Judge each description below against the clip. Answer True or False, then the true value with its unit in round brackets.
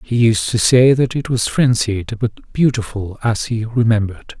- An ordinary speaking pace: True (175 wpm)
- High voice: False (115 Hz)